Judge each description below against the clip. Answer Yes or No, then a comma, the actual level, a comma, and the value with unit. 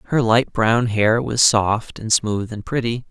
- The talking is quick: No, average, 195 wpm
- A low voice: Yes, low, 115 Hz